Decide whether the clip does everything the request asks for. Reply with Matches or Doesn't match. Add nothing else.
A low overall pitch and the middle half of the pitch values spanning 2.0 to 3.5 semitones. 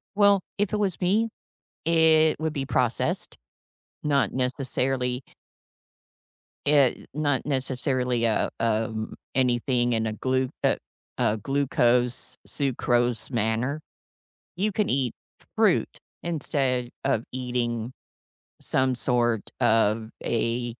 Matches